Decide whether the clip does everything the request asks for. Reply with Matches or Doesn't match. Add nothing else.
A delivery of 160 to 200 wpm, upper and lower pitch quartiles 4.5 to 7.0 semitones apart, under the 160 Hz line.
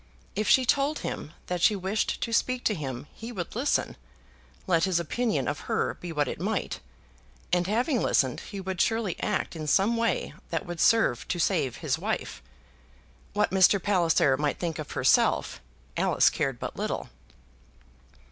Doesn't match